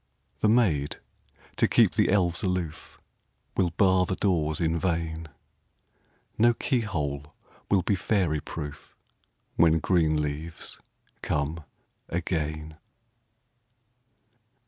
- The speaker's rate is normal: No, slow, 100 wpm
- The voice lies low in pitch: Yes, very low, 85 Hz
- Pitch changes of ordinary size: Yes, average, 3.4 semitones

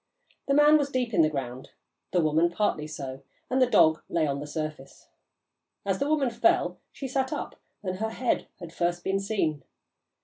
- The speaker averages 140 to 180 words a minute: No, average, 190 wpm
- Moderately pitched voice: Yes, medium, 180 Hz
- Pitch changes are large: Yes, wide, 8.6 semitones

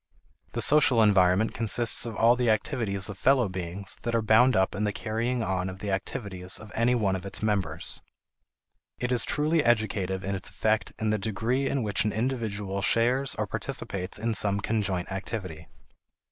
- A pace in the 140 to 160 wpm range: No, average, 180 wpm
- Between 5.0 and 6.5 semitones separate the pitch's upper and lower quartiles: No, average, 3.3 semitones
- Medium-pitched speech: No, low, 105 Hz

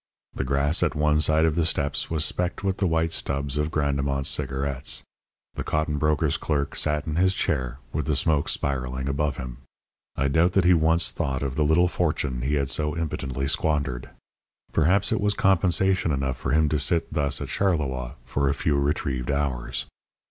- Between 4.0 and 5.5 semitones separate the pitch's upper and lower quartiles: No, average, 3.0 semitones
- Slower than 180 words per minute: No, average, 185 wpm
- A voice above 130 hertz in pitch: No, very low, 75 Hz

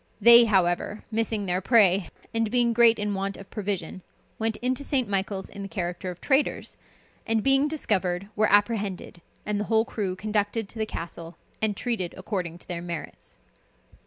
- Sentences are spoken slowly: No, average, 170 wpm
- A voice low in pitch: No, high, 205 Hz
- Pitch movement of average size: Yes, average, 3.4 semitones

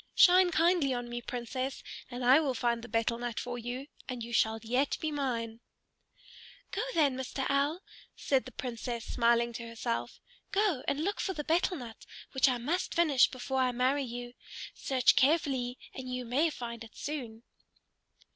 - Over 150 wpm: Yes, average, 175 wpm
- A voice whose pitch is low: No, very high, 255 Hz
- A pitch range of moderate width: Yes, average, 3.2 semitones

